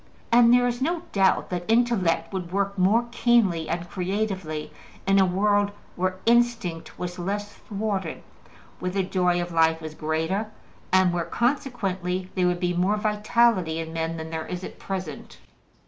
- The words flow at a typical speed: Yes, average, 160 wpm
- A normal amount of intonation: Yes, average, 3.4 semitones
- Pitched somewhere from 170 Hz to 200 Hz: Yes, medium, 185 Hz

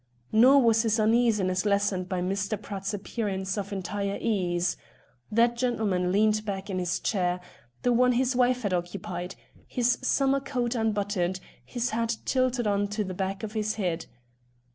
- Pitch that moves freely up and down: No, average, 3.7 semitones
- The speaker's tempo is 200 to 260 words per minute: No, average, 160 wpm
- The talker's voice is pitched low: No, high, 210 Hz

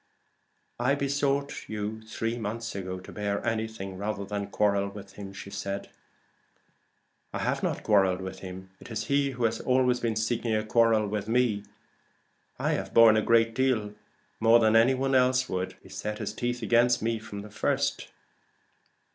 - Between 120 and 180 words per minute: Yes, average, 165 wpm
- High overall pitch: No, low, 110 Hz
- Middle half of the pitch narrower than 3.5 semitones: Yes, average, 2.8 semitones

